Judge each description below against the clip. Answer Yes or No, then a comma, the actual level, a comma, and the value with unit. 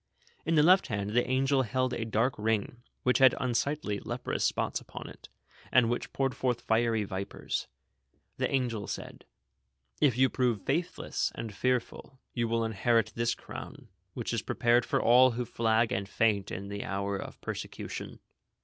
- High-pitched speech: No, low, 120 Hz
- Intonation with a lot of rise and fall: No, average, 2.9 semitones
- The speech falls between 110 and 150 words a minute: No, average, 165 wpm